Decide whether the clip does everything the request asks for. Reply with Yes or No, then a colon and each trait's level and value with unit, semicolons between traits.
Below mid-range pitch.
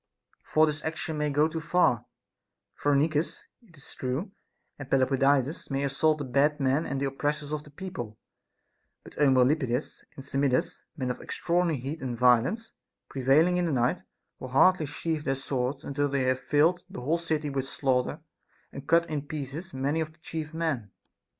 No: medium, 145 Hz